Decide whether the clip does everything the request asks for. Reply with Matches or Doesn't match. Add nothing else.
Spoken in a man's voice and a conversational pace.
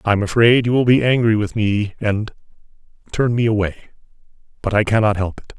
Matches